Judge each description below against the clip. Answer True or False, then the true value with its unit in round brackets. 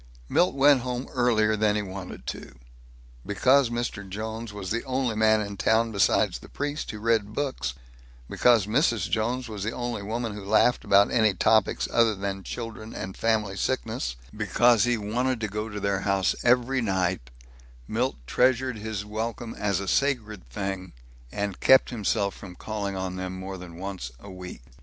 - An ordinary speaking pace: True (170 wpm)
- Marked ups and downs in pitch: False (3.2 semitones)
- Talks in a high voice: False (110 Hz)